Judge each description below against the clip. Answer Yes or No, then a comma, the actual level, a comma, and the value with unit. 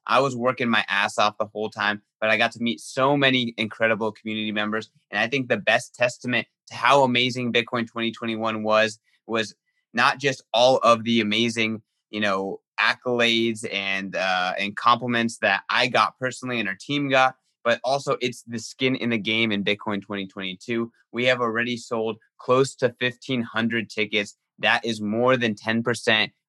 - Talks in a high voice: No, low, 115 Hz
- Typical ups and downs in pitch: No, narrow, 2.3 semitones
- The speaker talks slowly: No, average, 175 wpm